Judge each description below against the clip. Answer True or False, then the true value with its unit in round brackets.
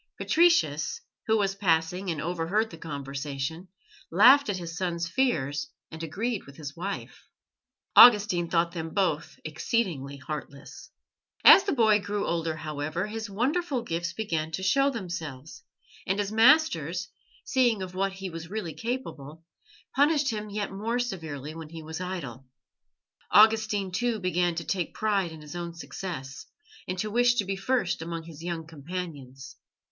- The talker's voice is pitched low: False (180 Hz)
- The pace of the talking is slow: False (150 wpm)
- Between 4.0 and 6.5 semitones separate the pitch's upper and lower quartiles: True (4.9 semitones)